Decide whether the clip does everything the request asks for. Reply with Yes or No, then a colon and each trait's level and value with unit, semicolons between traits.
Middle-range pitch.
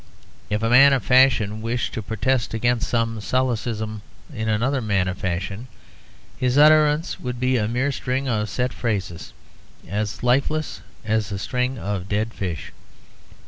No: low, 115 Hz